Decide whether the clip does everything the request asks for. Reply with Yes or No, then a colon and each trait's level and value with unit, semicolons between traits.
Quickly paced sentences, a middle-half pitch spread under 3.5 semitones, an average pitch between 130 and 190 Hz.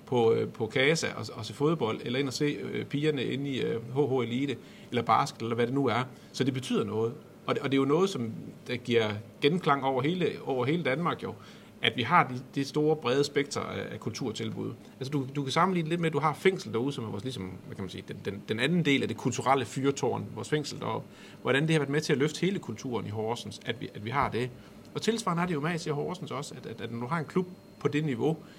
No: fast, 260 wpm; average, 4.1 semitones; medium, 140 Hz